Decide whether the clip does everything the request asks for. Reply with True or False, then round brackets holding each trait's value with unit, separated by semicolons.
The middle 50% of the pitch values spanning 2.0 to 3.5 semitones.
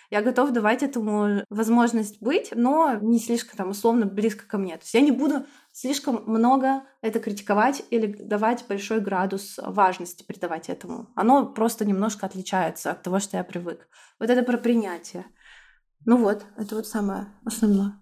True (2.8 semitones)